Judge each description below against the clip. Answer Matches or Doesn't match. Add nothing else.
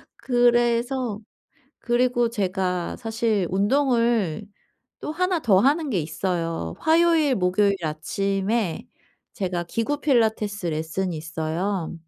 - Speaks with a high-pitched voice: Matches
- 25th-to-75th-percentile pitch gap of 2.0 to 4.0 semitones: Doesn't match